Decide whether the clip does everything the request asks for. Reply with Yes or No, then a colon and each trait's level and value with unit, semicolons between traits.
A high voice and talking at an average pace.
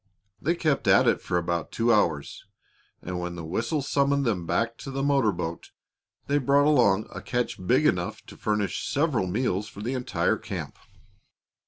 No: low, 115 Hz; average, 175 wpm